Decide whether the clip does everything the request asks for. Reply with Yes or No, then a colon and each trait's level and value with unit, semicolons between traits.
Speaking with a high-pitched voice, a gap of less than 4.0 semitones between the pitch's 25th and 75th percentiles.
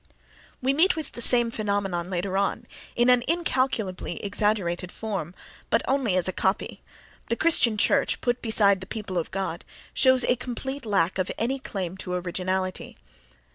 No: high, 205 Hz; average, 4.9 semitones